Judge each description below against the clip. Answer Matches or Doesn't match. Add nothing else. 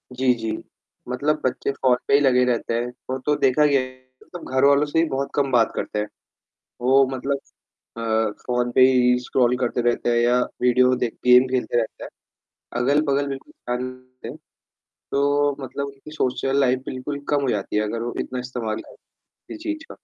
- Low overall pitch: Matches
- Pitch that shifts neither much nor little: Doesn't match